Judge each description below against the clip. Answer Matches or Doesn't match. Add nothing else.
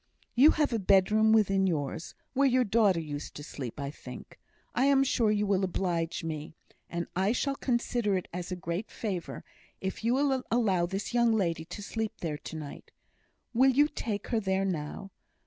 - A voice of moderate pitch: Doesn't match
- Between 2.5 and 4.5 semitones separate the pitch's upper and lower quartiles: Doesn't match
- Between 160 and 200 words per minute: Matches